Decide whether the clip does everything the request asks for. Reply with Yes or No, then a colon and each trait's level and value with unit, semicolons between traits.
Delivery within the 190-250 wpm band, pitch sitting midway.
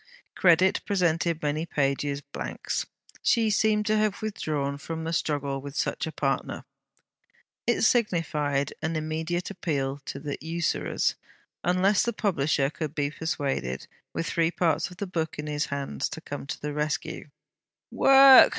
No: average, 150 wpm; medium, 160 Hz